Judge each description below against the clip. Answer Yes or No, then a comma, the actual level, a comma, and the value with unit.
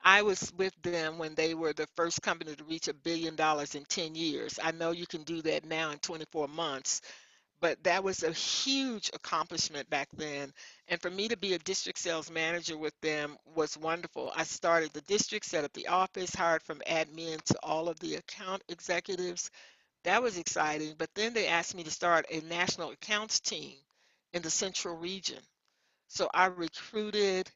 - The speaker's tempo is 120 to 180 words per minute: No, average, 190 wpm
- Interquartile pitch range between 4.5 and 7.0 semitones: No, average, 2.7 semitones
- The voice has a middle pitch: Yes, medium, 170 Hz